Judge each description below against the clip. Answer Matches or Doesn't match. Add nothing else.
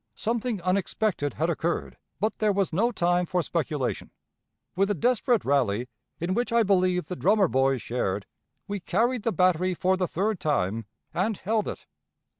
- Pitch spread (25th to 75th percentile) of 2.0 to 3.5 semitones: Doesn't match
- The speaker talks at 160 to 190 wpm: Matches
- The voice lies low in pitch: Doesn't match